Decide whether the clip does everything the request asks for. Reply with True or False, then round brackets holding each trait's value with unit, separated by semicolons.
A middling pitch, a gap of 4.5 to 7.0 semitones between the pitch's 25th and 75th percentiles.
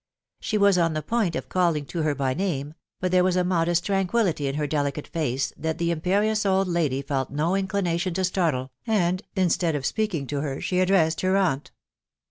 False (170 Hz; 4.1 semitones)